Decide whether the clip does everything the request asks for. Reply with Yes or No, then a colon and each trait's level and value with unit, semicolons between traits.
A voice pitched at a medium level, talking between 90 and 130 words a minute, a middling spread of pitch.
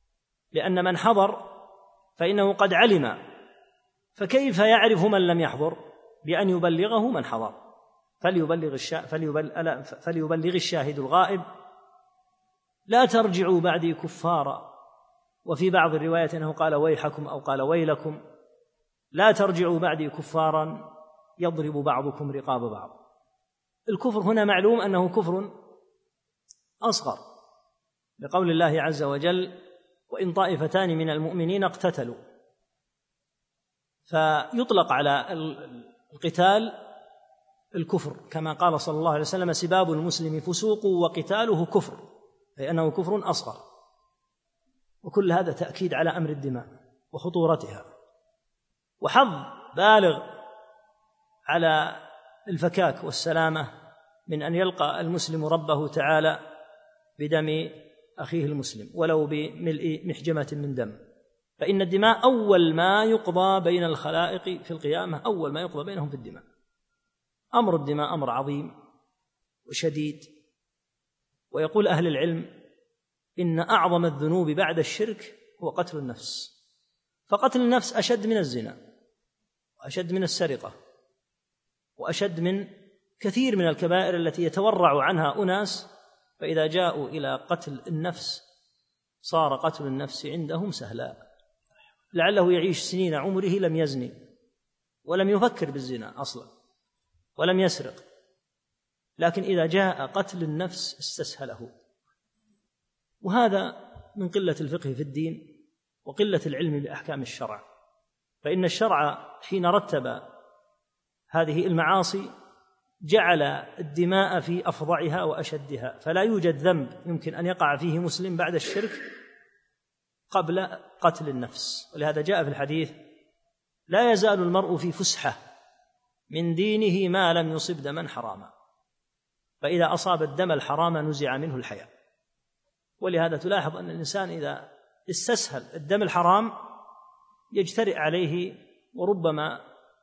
Yes: medium, 175 Hz; average, 105 wpm; average, 4.2 semitones